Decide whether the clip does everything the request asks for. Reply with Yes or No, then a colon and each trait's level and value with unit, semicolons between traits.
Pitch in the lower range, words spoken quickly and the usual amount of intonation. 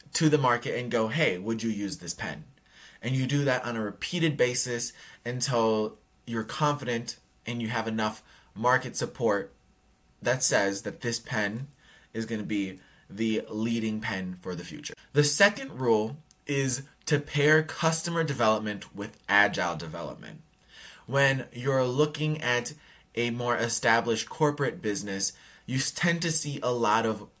No: low, 120 Hz; average, 155 wpm; average, 4.6 semitones